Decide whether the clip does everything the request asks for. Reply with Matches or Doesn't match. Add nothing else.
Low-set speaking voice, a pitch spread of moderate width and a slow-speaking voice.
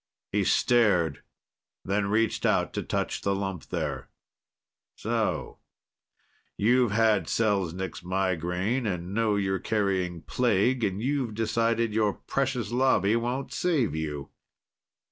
Matches